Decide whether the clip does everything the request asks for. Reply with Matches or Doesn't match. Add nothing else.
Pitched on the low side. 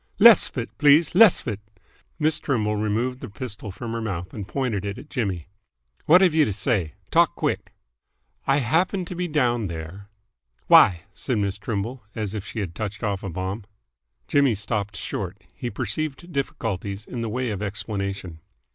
Matches